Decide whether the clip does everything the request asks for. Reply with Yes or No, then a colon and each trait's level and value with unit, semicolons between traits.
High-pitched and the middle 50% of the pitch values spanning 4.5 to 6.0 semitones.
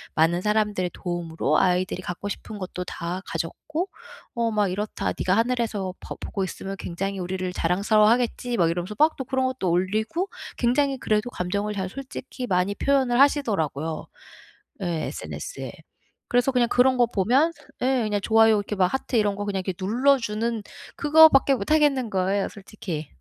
Yes: high, 210 Hz; average, 5.2 semitones